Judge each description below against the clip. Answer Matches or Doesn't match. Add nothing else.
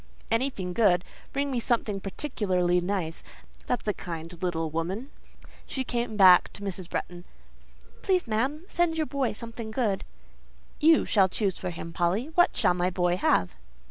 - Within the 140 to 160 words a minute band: Matches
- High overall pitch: Matches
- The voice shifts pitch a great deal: Matches